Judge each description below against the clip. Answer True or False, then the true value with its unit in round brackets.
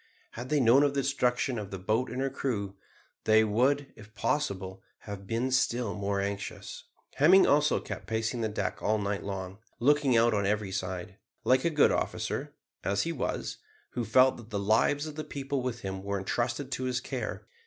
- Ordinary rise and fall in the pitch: True (4.9 semitones)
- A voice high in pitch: False (115 Hz)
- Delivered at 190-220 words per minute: True (195 wpm)